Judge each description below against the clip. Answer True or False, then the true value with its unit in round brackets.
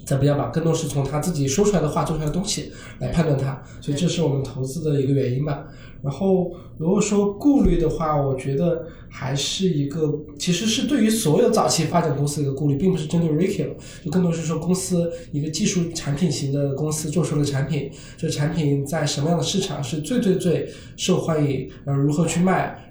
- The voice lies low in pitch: False (155 Hz)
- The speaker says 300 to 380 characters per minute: True (340 characters per minute)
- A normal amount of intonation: True (3.5 semitones)